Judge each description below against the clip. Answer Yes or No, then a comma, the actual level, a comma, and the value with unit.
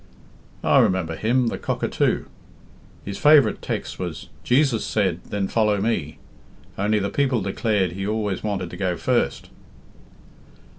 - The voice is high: No, low, 105 Hz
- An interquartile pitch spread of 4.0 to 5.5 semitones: No, average, 3.3 semitones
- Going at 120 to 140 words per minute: Yes, slow, 135 wpm